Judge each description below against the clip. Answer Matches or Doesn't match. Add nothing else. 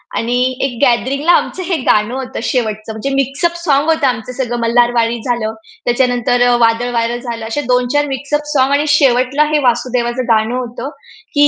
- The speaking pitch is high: Matches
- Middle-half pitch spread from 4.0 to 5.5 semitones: Doesn't match